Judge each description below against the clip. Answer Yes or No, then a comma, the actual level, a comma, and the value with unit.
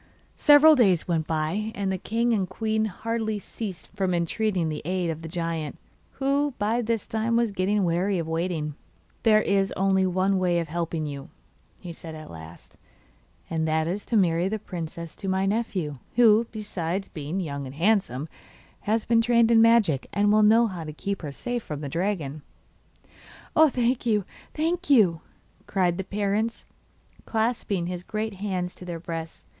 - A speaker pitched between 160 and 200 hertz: Yes, high, 190 Hz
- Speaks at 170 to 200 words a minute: Yes, average, 175 wpm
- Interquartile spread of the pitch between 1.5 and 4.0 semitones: No, average, 4.8 semitones